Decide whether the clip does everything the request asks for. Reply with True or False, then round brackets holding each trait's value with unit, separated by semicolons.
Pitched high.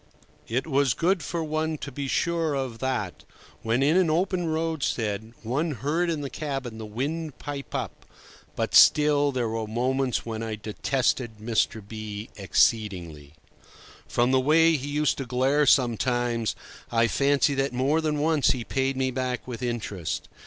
False (130 Hz)